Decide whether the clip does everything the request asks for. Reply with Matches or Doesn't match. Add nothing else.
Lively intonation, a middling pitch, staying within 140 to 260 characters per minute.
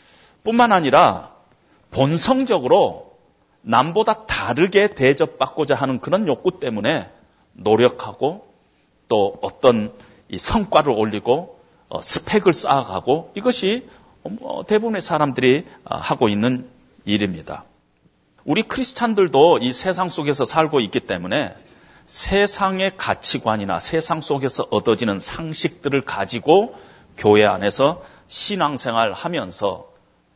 Matches